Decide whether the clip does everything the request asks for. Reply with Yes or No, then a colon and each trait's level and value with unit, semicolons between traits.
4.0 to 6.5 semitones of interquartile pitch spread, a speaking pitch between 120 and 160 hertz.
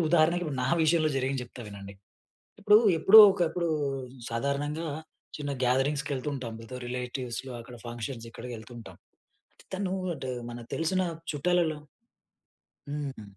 Yes: average, 4.6 semitones; low, 135 Hz